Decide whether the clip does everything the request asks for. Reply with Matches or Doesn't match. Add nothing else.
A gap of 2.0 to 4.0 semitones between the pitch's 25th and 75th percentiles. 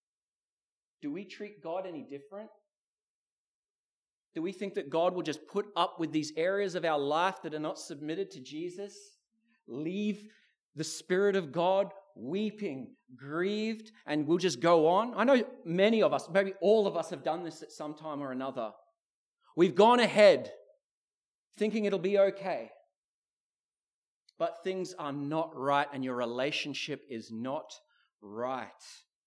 Doesn't match